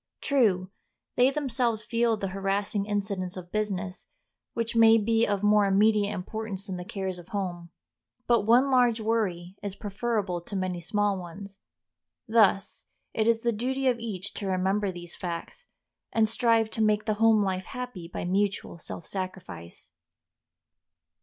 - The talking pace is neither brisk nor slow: Yes, average, 155 wpm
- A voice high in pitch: Yes, high, 205 Hz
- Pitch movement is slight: No, average, 3.2 semitones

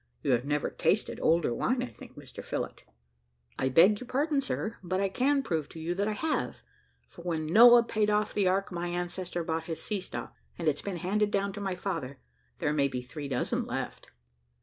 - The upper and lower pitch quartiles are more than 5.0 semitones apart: No, average, 4.7 semitones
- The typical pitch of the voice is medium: Yes, medium, 180 Hz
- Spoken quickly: Yes, fast, 210 wpm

